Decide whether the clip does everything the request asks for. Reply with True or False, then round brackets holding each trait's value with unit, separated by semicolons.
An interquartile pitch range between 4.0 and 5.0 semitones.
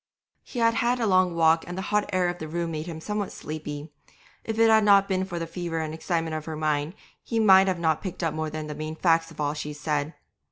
False (3.5 semitones)